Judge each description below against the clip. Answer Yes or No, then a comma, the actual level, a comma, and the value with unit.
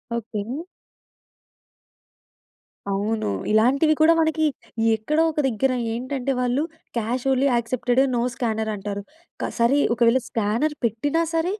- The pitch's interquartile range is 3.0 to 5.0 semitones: Yes, average, 4.1 semitones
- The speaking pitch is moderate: No, high, 245 Hz